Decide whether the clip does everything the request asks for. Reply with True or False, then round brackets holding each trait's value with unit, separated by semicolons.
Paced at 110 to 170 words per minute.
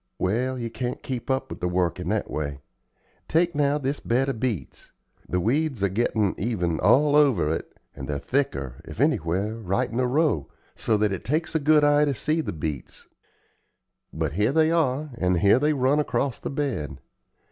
False (190 wpm)